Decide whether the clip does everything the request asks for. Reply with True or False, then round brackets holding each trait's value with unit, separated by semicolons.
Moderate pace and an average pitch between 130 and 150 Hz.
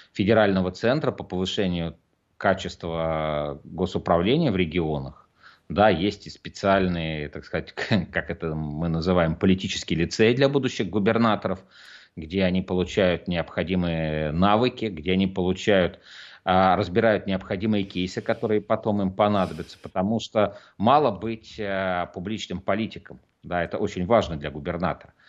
False (120 wpm; 95 Hz)